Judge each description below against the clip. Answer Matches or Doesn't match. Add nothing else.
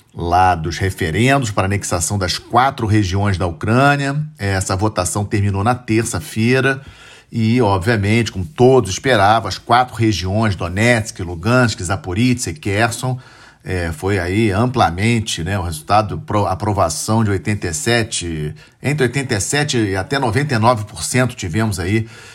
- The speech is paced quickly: Doesn't match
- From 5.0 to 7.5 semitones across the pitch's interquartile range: Doesn't match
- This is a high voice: Doesn't match